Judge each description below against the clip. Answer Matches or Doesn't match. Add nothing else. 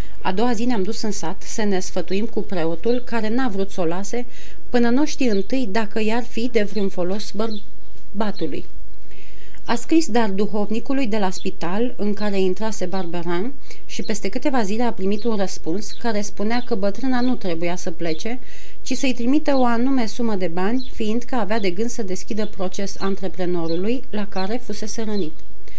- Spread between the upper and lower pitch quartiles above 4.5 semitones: Doesn't match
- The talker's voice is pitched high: Matches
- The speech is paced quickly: Matches